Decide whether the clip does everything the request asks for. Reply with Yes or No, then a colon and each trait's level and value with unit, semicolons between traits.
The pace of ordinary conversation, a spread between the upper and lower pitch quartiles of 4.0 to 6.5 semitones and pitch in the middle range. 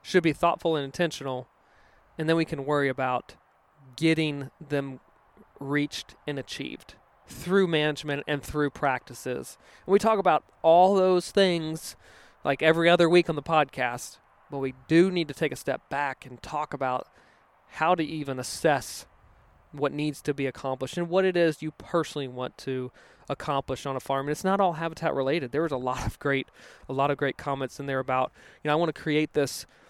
No: average, 190 wpm; average, 3.4 semitones; medium, 145 Hz